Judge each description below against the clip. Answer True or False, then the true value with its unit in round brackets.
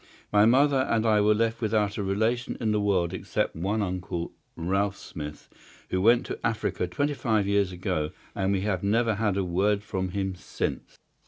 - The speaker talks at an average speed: True (185 wpm)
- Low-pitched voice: True (100 Hz)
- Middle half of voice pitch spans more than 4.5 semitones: False (3.0 semitones)